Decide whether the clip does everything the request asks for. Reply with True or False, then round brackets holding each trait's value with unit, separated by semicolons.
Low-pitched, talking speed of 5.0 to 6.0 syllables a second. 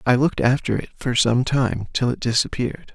True (125 Hz; 5.5 syllables/s)